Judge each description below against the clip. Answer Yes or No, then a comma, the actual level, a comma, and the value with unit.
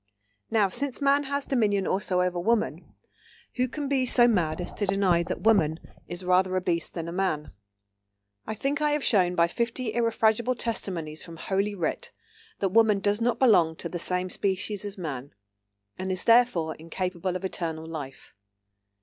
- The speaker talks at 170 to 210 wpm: Yes, average, 175 wpm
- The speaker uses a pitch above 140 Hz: Yes, high, 190 Hz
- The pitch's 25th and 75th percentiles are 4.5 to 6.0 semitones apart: Yes, average, 5.0 semitones